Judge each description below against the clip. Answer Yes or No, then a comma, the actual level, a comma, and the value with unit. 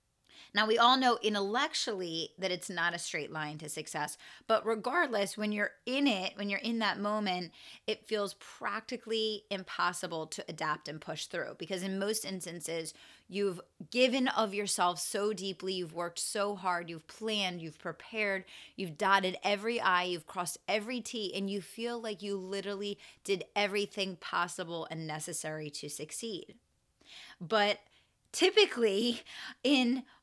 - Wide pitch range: No, average, 3.8 semitones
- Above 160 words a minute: No, average, 150 wpm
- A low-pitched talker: No, high, 200 Hz